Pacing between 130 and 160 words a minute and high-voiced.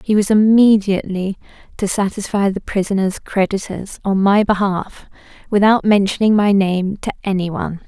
Yes: slow, 135 wpm; high, 200 Hz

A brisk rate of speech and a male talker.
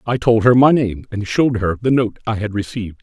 Yes: fast, 260 wpm; male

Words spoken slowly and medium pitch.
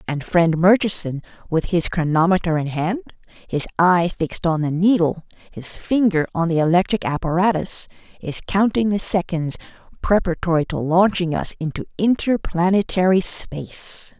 Yes: slow, 130 wpm; medium, 175 Hz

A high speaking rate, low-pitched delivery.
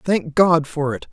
No: fast, 215 wpm; medium, 165 Hz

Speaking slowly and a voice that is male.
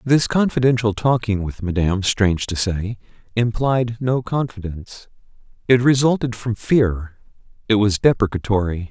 Yes: slow, 115 wpm; male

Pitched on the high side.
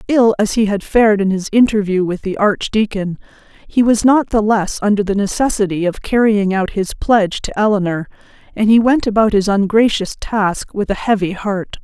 Yes: high, 205 Hz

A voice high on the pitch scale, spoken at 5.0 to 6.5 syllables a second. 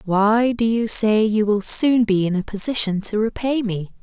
No: high, 215 Hz; 4.5 syllables/s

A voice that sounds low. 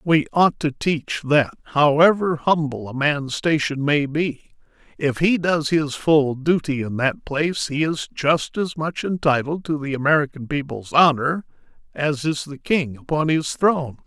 No: medium, 150 Hz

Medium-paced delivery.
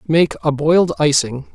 Yes: average, 155 wpm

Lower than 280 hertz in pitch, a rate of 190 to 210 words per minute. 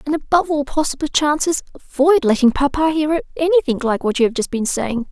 No: very high, 285 Hz; average, 200 wpm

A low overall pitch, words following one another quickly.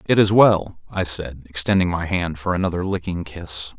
No: very low, 85 Hz; average, 190 wpm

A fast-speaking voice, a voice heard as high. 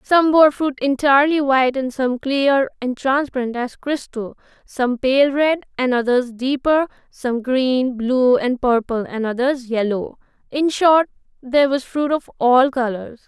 No: average, 155 wpm; very high, 260 Hz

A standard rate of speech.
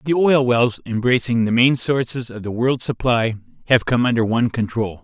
Yes: average, 190 wpm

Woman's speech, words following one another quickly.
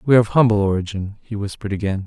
No: male; fast, 230 wpm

